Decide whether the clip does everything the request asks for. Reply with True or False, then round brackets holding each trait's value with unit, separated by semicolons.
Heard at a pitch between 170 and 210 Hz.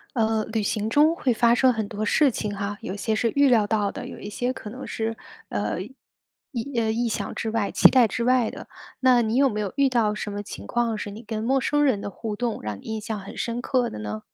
False (225 Hz)